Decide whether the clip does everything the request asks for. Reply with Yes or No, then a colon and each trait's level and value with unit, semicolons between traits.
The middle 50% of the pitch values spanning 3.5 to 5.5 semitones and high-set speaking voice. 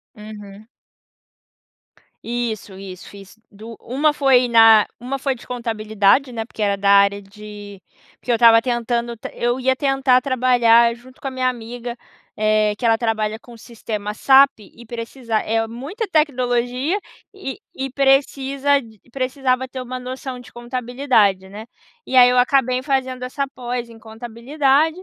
No: average, 2.8 semitones; high, 240 Hz